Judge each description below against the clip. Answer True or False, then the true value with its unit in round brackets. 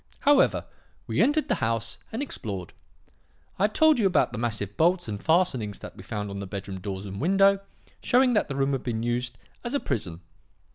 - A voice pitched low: True (120 Hz)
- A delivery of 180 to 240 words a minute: True (200 wpm)